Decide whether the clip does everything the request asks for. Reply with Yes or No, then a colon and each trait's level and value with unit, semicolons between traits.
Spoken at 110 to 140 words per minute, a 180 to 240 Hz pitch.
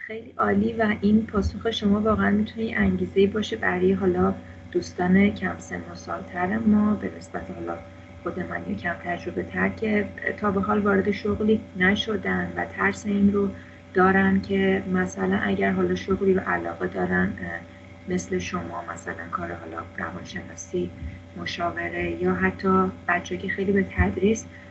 No: average, 150 wpm; medium, 185 Hz